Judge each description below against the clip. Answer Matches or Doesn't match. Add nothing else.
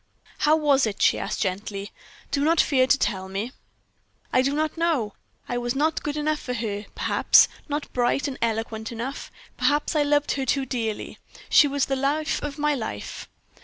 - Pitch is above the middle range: Matches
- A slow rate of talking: Doesn't match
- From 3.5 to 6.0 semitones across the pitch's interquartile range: Matches